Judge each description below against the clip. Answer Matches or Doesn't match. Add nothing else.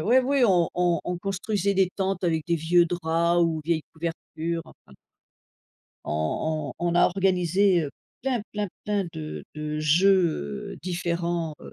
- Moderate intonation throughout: Matches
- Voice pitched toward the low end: Doesn't match